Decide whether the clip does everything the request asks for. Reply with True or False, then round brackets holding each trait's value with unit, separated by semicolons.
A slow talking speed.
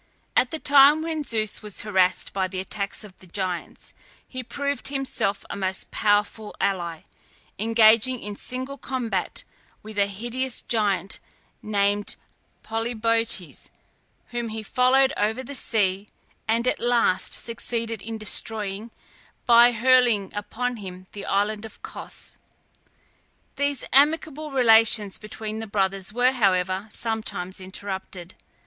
True (125 wpm)